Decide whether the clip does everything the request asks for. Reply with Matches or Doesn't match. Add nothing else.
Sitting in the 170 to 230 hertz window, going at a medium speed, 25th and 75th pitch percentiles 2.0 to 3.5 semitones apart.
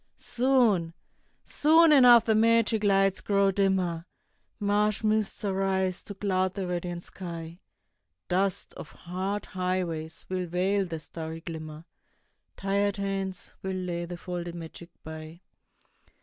Doesn't match